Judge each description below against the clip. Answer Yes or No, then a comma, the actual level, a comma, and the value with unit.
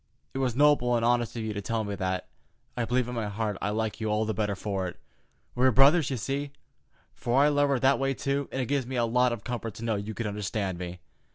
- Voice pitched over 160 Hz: No, low, 115 Hz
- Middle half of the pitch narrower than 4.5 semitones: Yes, average, 4.0 semitones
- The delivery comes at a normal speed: No, fast, 265 wpm